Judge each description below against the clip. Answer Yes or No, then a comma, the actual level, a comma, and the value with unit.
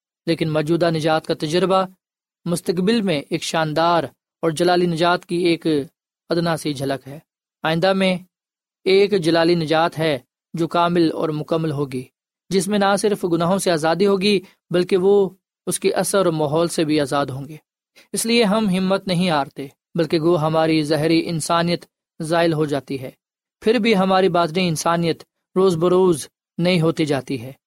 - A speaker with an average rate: Yes, average, 165 wpm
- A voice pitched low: No, medium, 170 Hz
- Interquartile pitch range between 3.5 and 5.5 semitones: No, average, 3.0 semitones